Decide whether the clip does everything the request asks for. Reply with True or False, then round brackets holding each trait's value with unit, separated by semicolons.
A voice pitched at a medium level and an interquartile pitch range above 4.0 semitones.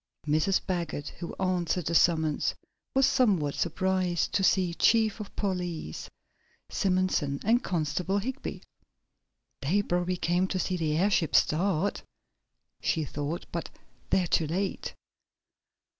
False (180 Hz; 3.1 semitones)